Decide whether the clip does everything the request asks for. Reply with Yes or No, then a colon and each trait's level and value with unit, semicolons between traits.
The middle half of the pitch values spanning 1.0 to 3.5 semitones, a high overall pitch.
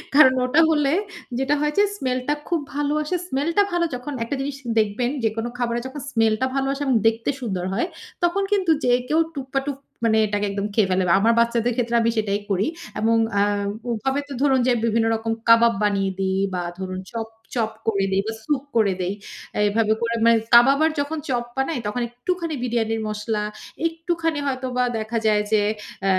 No: average, 4.3 semitones; high, 235 Hz